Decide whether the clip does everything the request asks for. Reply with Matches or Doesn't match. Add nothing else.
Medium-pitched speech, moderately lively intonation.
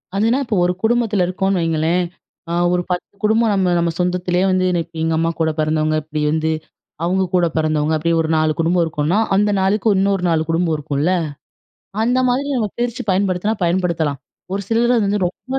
Matches